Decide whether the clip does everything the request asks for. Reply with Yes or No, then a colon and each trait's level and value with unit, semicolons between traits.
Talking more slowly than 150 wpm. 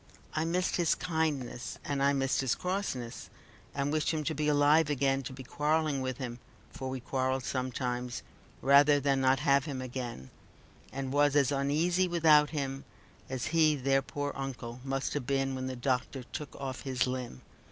No: average, 175 wpm